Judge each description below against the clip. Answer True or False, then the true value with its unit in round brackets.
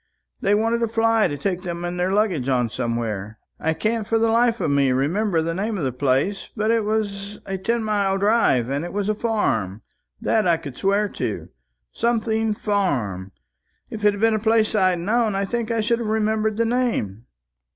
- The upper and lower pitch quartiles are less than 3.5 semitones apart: False (5.6 semitones)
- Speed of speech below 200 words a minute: False (205 wpm)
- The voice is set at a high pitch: True (205 Hz)